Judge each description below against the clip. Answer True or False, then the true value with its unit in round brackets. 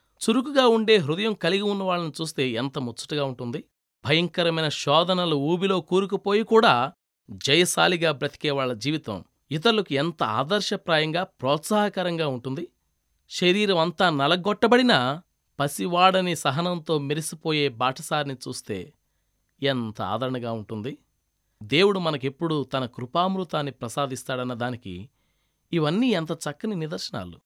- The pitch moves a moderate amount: False (5.8 semitones)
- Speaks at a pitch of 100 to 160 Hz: True (155 Hz)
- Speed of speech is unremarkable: True (95 wpm)